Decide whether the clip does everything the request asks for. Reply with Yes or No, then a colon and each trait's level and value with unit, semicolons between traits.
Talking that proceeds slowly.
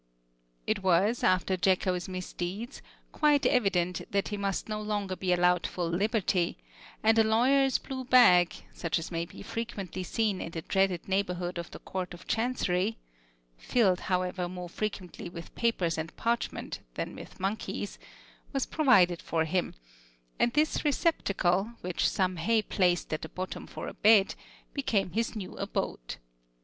No: average, 155 wpm